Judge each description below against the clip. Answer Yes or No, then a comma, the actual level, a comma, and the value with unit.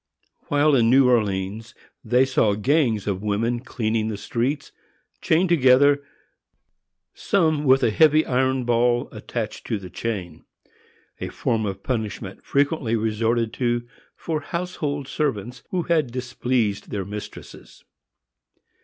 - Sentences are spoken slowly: Yes, slow, 125 wpm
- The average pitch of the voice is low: Yes, low, 120 Hz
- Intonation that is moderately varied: Yes, average, 4.6 semitones